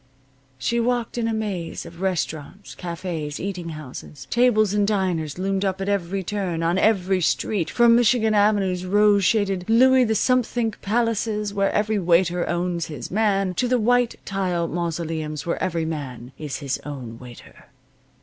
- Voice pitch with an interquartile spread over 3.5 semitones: Yes, average, 4.3 semitones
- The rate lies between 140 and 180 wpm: Yes, average, 160 wpm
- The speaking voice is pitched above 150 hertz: Yes, high, 190 Hz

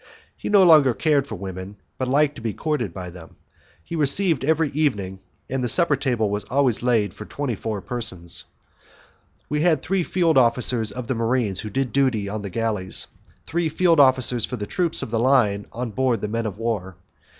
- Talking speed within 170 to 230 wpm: Yes, average, 200 wpm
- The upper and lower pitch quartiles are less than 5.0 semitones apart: No, wide, 5.5 semitones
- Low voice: Yes, low, 125 Hz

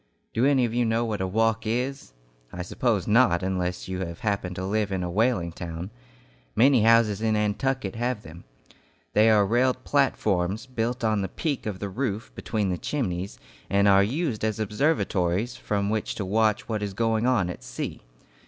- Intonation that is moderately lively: Yes, average, 3.8 semitones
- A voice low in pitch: Yes, low, 105 Hz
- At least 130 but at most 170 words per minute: No, average, 185 wpm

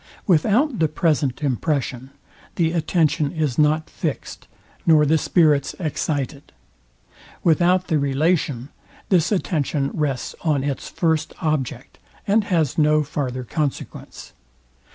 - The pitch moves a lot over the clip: No, average, 2.9 semitones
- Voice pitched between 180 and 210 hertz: No, medium, 155 Hz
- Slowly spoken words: Yes, slow, 110 wpm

